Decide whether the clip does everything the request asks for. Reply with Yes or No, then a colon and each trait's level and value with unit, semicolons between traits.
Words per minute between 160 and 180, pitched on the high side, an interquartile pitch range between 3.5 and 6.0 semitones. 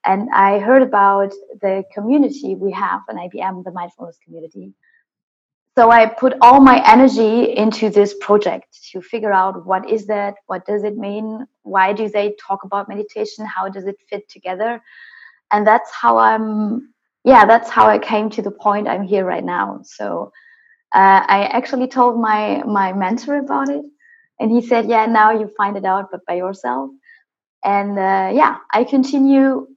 Yes: average, 175 wpm; high, 215 Hz; average, 3.8 semitones